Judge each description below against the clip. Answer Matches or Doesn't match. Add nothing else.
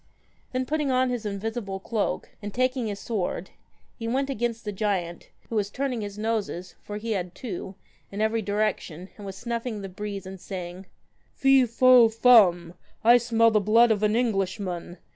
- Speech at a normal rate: Matches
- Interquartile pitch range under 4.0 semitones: Matches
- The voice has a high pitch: Matches